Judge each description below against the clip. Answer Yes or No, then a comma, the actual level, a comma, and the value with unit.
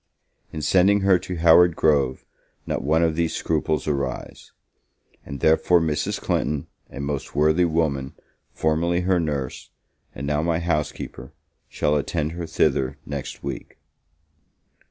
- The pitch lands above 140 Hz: No, very low, 80 Hz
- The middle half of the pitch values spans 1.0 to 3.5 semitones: Yes, average, 2.9 semitones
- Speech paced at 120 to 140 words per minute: Yes, slow, 135 wpm